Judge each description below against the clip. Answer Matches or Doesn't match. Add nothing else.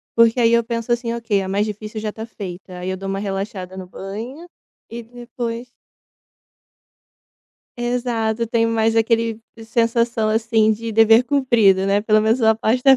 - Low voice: Doesn't match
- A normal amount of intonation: Doesn't match